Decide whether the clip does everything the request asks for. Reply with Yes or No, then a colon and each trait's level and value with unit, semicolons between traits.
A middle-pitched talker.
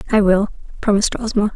No: high, 205 Hz